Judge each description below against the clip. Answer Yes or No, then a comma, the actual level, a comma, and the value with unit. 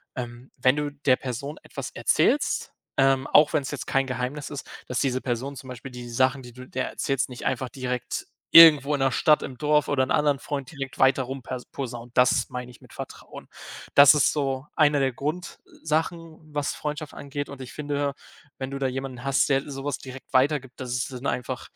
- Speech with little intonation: Yes, narrow, 2.2 semitones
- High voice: No, low, 135 Hz